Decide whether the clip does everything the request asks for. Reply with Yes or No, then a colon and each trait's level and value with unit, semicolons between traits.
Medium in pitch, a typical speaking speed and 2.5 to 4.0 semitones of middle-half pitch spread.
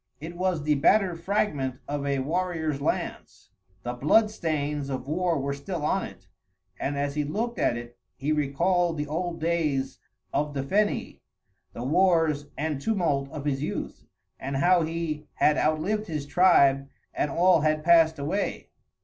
Yes: medium, 155 Hz; average, 160 wpm; average, 3.7 semitones